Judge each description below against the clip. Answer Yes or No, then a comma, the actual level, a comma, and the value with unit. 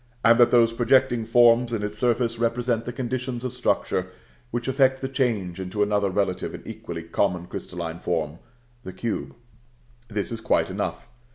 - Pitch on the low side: Yes, low, 115 Hz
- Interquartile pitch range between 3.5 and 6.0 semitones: Yes, average, 4.2 semitones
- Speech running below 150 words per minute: No, average, 165 wpm